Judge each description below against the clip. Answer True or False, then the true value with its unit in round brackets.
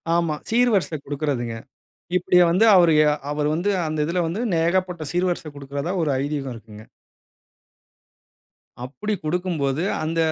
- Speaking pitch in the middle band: True (165 Hz)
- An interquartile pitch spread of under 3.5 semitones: False (3.8 semitones)